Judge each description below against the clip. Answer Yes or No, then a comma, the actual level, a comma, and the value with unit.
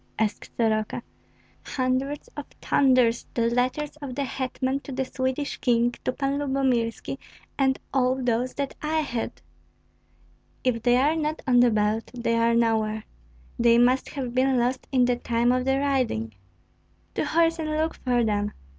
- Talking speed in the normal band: Yes, average, 160 wpm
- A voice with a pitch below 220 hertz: No, very high, 255 Hz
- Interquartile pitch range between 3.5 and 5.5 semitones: No, average, 2.7 semitones